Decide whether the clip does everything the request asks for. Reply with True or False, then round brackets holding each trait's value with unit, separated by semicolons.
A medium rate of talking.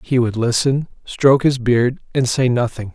True (185 wpm)